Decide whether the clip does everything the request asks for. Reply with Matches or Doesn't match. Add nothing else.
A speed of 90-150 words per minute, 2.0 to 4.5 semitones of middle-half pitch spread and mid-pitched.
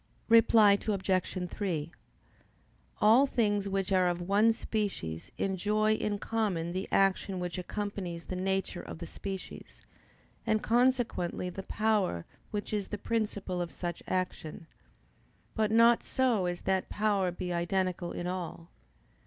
Doesn't match